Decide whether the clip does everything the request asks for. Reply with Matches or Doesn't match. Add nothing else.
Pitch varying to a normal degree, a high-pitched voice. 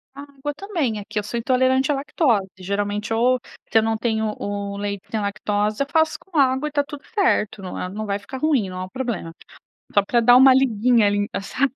Matches